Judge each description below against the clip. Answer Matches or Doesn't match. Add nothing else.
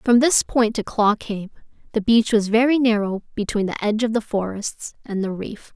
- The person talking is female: Matches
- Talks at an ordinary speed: Doesn't match